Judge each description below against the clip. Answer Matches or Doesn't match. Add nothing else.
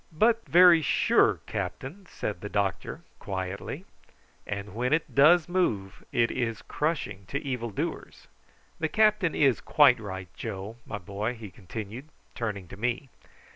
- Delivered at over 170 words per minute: Doesn't match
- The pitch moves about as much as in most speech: Doesn't match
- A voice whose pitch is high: Doesn't match